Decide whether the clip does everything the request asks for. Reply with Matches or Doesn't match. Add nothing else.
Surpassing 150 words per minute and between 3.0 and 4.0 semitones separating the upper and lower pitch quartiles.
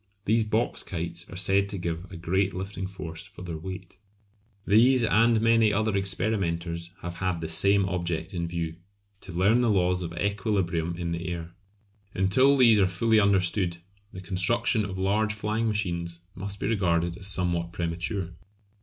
Matches